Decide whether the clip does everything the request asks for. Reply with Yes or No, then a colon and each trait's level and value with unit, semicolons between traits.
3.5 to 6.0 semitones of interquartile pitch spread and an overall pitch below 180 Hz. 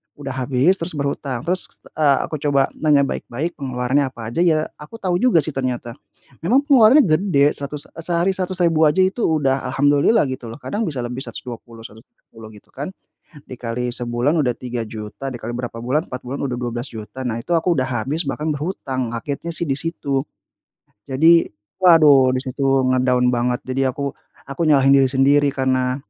Yes: average, 4.1 semitones; low, 135 Hz